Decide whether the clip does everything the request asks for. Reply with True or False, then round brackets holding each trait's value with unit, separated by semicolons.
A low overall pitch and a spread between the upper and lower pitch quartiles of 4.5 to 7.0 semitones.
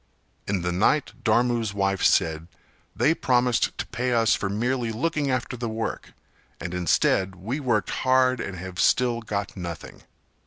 True (115 Hz; 4.8 semitones)